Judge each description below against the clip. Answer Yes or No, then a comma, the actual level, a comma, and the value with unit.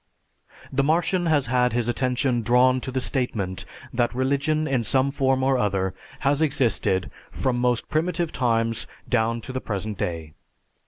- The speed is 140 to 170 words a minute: Yes, average, 155 wpm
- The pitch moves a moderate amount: Yes, average, 3.1 semitones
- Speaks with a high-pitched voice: No, low, 125 Hz